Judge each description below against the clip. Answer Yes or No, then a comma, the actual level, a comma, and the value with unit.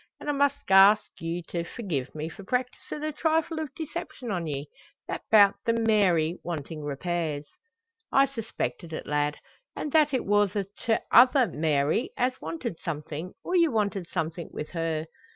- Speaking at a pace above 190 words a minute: No, average, 165 wpm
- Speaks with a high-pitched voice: Yes, high, 195 Hz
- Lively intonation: Yes, wide, 7.8 semitones